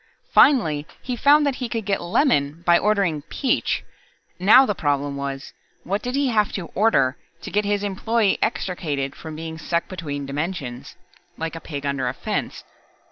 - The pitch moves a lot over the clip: Yes, wide, 6.7 semitones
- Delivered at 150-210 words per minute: Yes, average, 170 wpm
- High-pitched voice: No, medium, 175 Hz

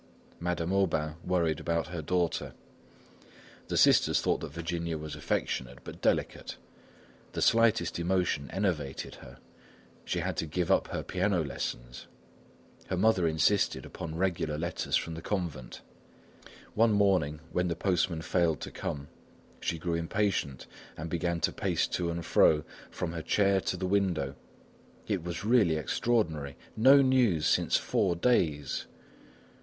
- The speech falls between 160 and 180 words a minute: No, average, 140 wpm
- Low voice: Yes, very low, 85 Hz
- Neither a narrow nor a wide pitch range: Yes, average, 3.4 semitones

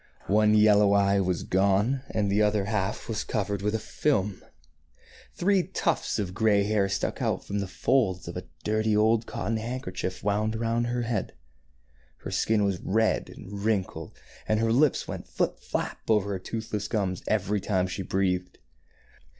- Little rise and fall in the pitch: Yes, narrow, 2.2 semitones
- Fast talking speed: No, average, 170 wpm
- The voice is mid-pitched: No, low, 105 Hz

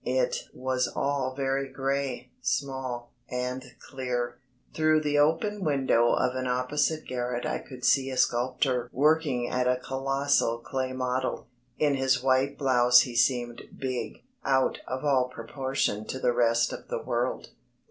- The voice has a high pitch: No, low, 130 Hz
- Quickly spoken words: No, average, 145 wpm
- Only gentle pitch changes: Yes, narrow, 1.8 semitones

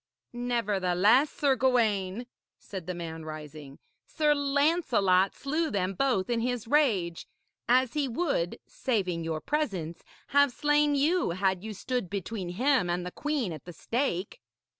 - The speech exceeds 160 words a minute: No, average, 140 wpm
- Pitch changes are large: Yes, wide, 7.4 semitones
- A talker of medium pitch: No, high, 225 Hz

